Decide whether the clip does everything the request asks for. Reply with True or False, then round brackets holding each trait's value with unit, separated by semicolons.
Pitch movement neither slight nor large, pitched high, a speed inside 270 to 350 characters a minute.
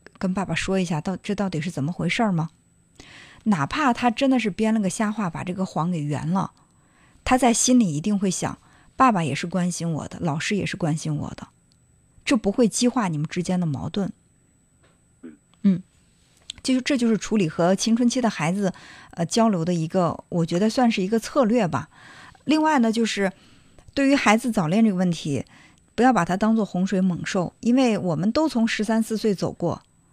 True (4.7 semitones; 195 Hz; 275 characters per minute)